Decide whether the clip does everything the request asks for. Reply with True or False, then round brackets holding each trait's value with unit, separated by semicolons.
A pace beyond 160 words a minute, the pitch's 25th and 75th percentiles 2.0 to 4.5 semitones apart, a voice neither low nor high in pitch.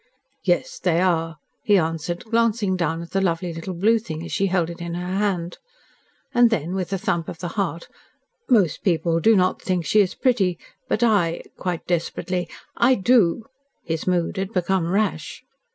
True (185 wpm; 3.0 semitones; 180 Hz)